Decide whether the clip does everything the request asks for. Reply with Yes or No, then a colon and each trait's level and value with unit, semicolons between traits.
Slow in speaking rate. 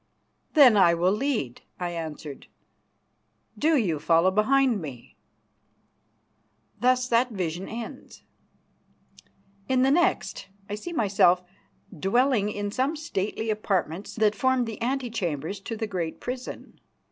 Yes: slow, 120 wpm